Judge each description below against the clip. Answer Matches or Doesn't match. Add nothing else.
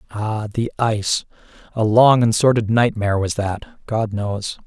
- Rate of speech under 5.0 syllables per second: Matches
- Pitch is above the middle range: Doesn't match